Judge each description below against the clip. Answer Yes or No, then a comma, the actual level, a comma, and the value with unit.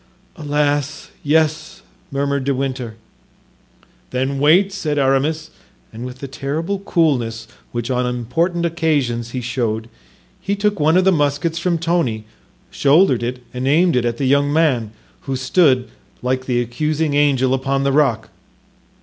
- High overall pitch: No, medium, 140 Hz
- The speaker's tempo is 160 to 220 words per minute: No, average, 140 wpm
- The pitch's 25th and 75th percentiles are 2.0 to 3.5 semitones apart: No, average, 4.1 semitones